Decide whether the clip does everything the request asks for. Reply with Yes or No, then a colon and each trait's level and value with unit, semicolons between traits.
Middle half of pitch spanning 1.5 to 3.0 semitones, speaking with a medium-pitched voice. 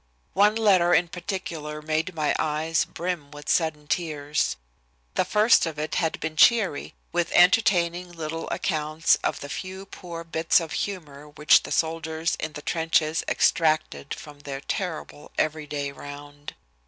Yes: average, 2.7 semitones; medium, 160 Hz